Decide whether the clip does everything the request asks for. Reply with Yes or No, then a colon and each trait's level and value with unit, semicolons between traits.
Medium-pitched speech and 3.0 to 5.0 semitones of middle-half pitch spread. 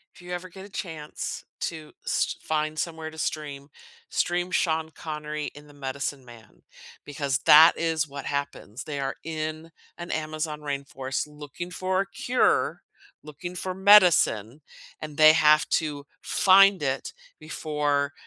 No: medium, 155 Hz; narrow, 2.6 semitones